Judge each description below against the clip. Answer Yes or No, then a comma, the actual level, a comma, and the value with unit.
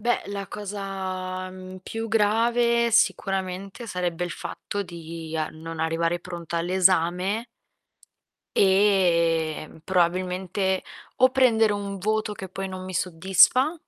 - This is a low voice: No, medium, 185 Hz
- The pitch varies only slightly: No, average, 3.0 semitones